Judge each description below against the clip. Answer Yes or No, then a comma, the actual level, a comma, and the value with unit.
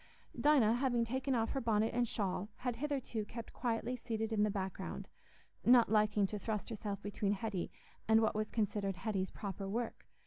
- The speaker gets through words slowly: No, average, 175 wpm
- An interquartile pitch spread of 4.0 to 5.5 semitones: No, narrow, 2.5 semitones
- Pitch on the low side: No, high, 220 Hz